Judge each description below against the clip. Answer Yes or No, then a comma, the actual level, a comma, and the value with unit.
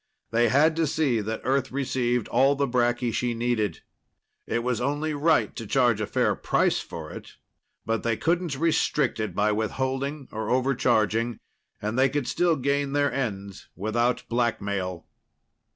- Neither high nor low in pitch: No, low, 125 Hz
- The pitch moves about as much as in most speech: Yes, average, 3.9 semitones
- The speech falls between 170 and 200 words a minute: No, average, 155 wpm